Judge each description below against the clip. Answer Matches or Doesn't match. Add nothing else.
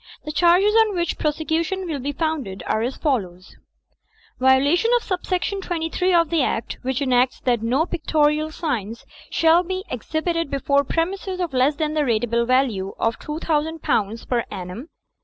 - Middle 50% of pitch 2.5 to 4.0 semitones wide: Doesn't match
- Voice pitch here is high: Matches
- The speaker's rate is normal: Matches